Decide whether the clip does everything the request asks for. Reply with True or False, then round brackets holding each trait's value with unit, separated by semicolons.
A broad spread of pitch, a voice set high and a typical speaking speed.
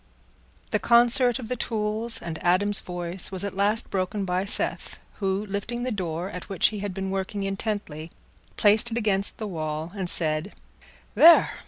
False (3.1 semitones; 200 Hz; 170 wpm)